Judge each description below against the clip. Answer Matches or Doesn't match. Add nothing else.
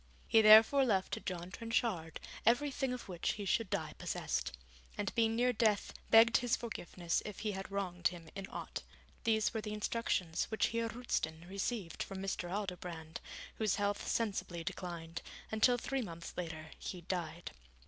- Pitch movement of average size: Matches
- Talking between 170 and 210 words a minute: Doesn't match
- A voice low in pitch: Doesn't match